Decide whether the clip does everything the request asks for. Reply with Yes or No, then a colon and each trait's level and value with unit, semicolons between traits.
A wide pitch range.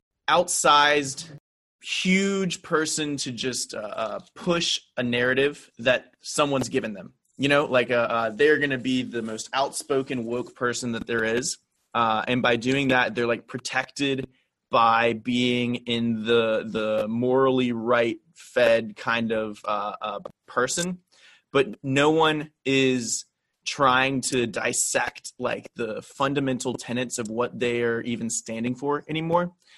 No: average, 3.4 semitones